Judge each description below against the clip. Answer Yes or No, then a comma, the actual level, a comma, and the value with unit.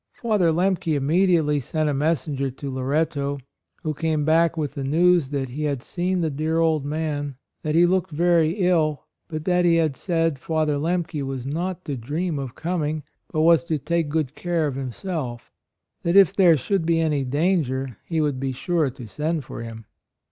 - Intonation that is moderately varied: Yes, average, 3.3 semitones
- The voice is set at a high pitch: No, medium, 155 Hz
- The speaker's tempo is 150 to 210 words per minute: Yes, average, 185 wpm